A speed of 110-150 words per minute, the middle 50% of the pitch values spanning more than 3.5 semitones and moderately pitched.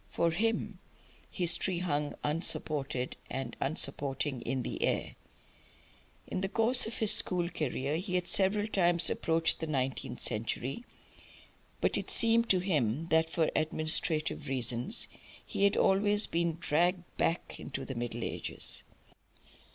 Yes: slow, 135 wpm; average, 5.3 semitones; medium, 165 Hz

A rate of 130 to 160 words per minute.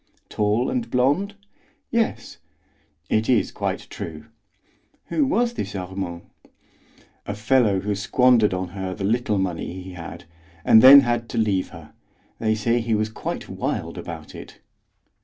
Yes: average, 145 wpm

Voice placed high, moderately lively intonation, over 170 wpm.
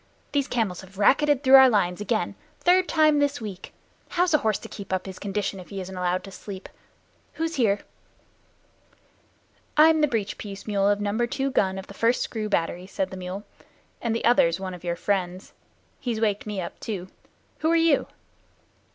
No: high, 205 Hz; wide, 5.8 semitones; average, 190 wpm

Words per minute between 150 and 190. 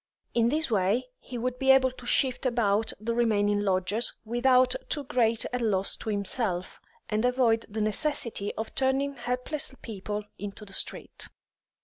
Yes: average, 155 wpm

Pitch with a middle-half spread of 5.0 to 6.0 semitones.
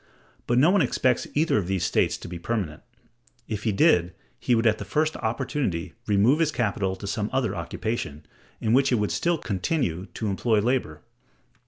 Yes: wide, 5.4 semitones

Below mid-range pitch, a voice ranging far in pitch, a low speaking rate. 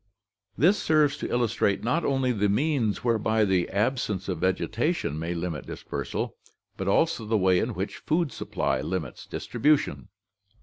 No: low, 110 Hz; wide, 6.6 semitones; average, 145 wpm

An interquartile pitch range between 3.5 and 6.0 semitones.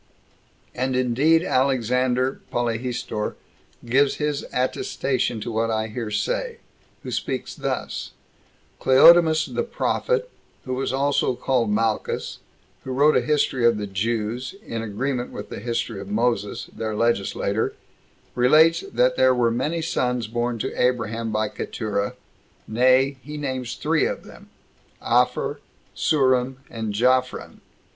No: average, 2.8 semitones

